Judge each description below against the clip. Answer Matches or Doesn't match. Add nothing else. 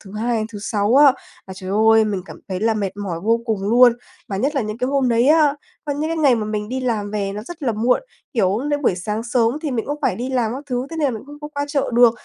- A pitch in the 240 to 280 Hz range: Doesn't match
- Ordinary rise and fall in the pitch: Matches